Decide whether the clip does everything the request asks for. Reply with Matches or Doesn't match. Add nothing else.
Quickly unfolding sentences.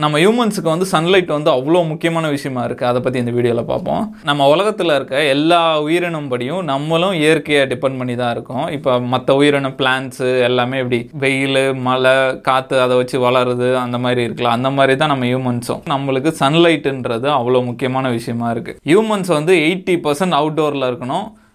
Matches